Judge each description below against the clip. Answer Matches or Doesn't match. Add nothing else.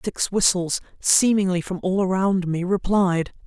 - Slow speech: Matches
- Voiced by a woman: Matches